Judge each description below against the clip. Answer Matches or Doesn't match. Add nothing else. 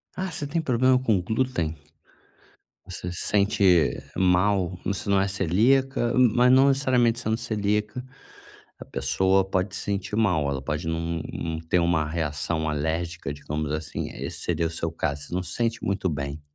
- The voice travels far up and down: Matches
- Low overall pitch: Matches